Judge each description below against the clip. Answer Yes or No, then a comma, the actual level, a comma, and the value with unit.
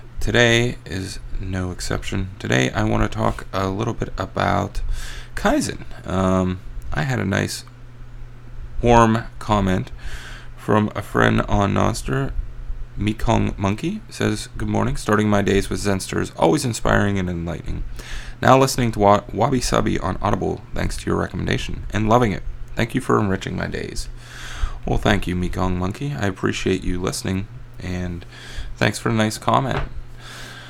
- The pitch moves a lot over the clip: No, average, 4.0 semitones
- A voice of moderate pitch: No, low, 105 Hz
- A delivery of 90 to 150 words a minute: Yes, average, 145 wpm